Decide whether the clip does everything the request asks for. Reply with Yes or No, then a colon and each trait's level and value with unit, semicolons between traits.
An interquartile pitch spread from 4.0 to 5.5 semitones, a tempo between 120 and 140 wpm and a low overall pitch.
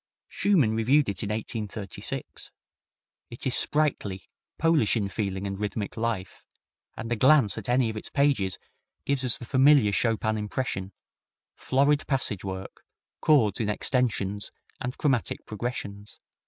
Yes: average, 4.4 semitones; slow, 135 wpm; low, 110 Hz